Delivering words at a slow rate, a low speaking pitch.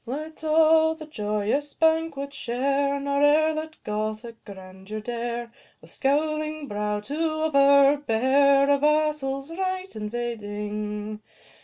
No: slow, 110 wpm; very high, 275 Hz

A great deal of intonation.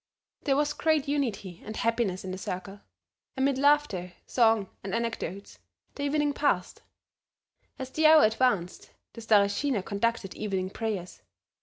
Yes: wide, 6.3 semitones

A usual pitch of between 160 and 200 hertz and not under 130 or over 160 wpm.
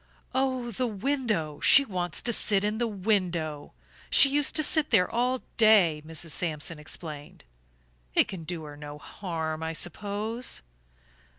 Yes: high, 190 Hz; average, 150 wpm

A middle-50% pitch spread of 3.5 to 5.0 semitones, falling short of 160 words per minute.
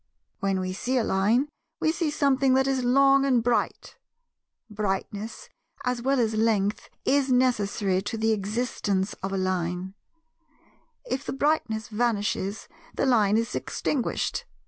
Yes: average, 4.6 semitones; average, 140 wpm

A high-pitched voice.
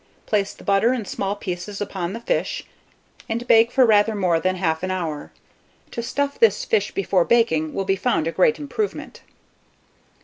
Yes: high, 205 Hz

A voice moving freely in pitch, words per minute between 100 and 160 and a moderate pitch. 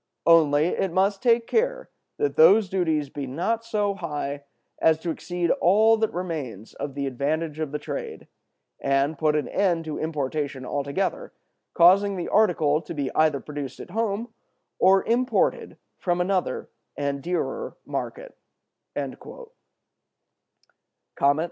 Yes: wide, 5.7 semitones; slow, 135 wpm; medium, 170 Hz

